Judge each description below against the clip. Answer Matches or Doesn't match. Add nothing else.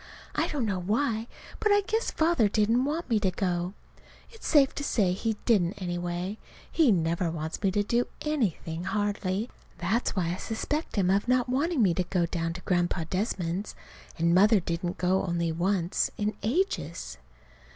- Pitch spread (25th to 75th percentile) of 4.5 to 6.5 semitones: Matches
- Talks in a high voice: Matches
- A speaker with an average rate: Matches